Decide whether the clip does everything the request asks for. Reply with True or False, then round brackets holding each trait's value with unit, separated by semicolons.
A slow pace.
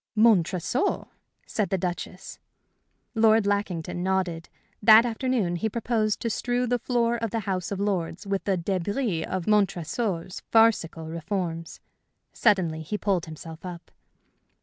True (130 wpm)